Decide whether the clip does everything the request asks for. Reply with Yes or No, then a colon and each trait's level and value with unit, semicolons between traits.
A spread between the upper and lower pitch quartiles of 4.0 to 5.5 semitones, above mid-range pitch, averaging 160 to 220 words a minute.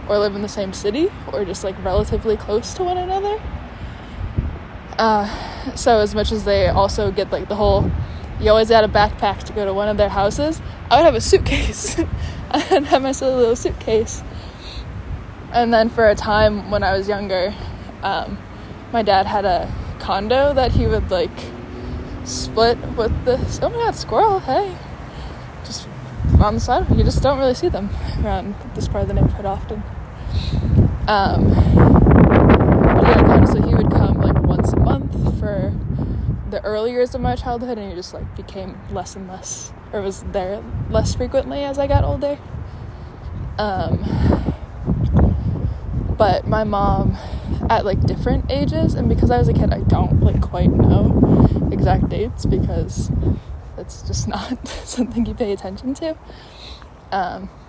Yes: average, 4.5 semitones; high, 225 Hz; average, 165 wpm